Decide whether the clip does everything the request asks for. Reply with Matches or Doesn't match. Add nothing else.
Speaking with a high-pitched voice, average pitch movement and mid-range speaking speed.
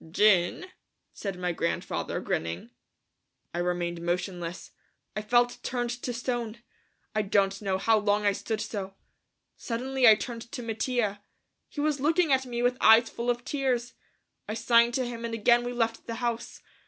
Matches